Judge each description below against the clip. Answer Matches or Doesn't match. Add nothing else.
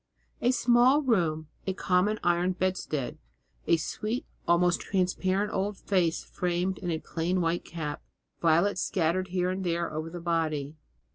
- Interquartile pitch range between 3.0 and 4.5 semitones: Doesn't match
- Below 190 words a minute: Matches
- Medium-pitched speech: Matches